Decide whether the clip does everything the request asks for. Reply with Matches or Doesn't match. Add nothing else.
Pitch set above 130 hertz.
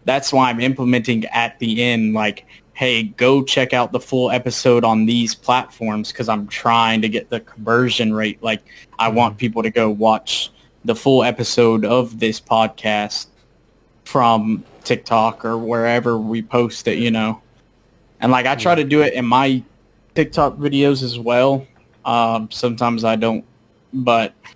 Doesn't match